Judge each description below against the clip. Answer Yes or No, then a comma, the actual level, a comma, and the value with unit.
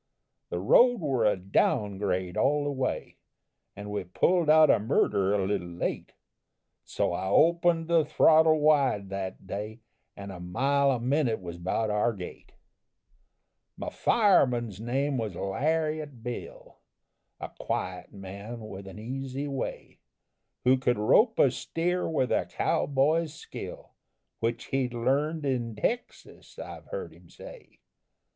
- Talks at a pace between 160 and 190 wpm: No, average, 140 wpm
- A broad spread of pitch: Yes, wide, 7.1 semitones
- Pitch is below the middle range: Yes, low, 125 Hz